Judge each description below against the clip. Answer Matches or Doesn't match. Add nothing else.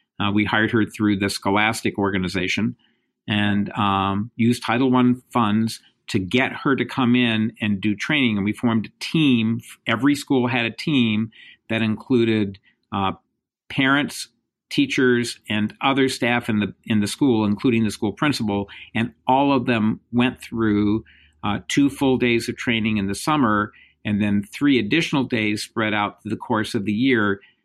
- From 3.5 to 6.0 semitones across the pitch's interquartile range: Doesn't match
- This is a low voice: Matches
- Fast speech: Doesn't match